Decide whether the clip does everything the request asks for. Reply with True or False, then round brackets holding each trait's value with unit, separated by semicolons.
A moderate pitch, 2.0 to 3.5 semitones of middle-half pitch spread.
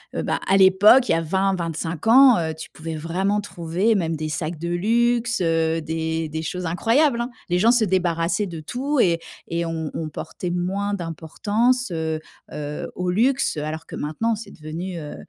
False (175 Hz; 4.7 semitones)